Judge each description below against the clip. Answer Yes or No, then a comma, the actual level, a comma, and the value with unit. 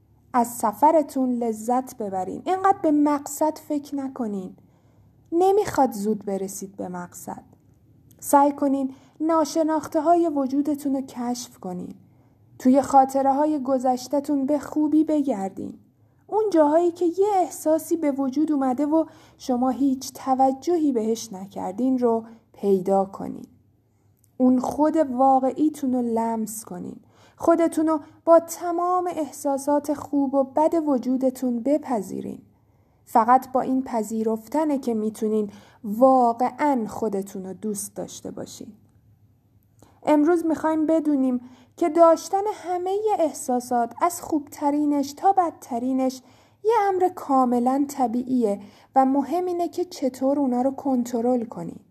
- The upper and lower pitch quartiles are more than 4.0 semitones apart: Yes, average, 4.7 semitones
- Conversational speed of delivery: Yes, average, 115 wpm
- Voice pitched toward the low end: No, very high, 270 Hz